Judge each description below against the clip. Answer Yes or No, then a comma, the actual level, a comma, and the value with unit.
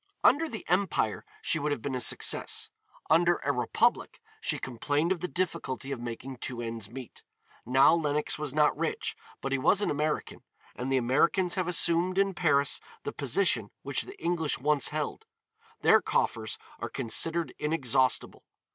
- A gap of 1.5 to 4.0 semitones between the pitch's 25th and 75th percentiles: No, average, 4.7 semitones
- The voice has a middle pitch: Yes, medium, 150 Hz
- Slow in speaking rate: No, average, 165 wpm